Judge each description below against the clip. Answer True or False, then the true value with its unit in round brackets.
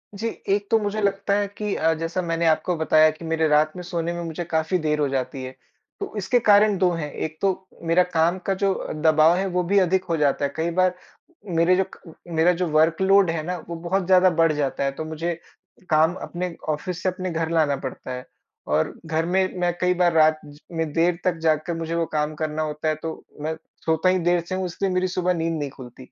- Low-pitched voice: False (165 Hz)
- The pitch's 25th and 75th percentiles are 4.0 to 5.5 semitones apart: False (2.7 semitones)